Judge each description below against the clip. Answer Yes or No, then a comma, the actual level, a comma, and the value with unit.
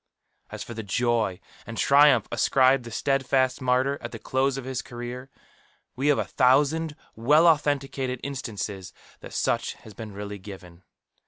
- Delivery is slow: No, average, 160 wpm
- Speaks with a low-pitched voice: Yes, low, 130 Hz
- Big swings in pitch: No, average, 3.4 semitones